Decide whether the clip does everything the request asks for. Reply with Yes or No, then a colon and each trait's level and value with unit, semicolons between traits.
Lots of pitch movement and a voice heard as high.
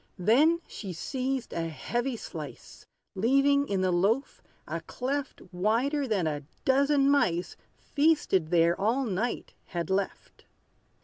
Yes: wide, 7.0 semitones; high, 235 Hz